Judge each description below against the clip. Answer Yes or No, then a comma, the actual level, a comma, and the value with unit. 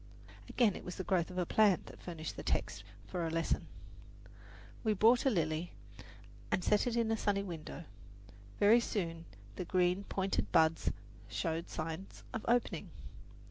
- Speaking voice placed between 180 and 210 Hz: Yes, medium, 185 Hz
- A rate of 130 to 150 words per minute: No, average, 160 wpm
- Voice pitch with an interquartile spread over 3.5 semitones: Yes, average, 4.2 semitones